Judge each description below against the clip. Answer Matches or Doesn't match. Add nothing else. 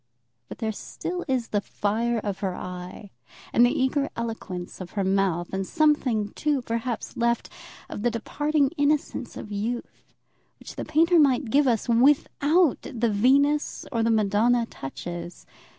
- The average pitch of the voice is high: Matches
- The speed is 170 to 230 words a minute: Doesn't match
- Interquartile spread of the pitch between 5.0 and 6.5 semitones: Matches